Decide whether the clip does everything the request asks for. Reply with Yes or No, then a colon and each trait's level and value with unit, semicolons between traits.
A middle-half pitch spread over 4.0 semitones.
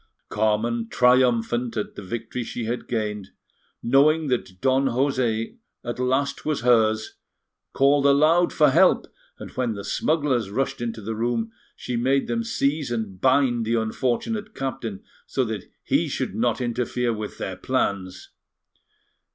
No: average, 3.4 semitones